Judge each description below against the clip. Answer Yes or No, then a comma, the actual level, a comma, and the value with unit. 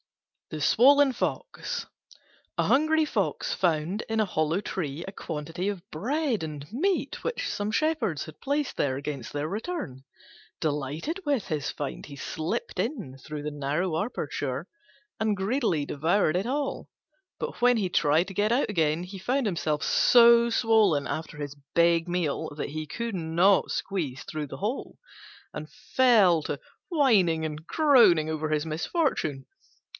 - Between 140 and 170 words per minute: Yes, average, 150 wpm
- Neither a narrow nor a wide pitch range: No, wide, 7.5 semitones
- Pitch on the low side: No, medium, 175 Hz